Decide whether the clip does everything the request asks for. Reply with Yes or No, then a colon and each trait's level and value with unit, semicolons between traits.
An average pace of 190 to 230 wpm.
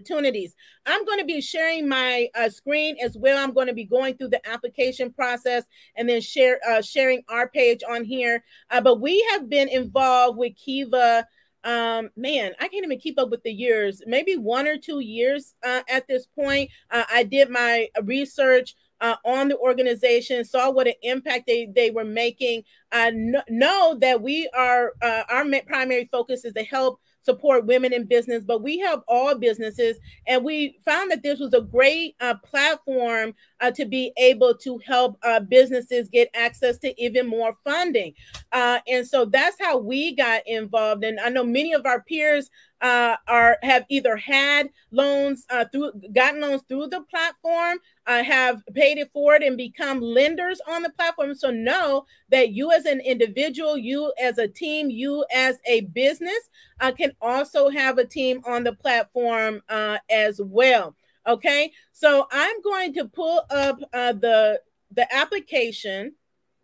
No: average, 175 wpm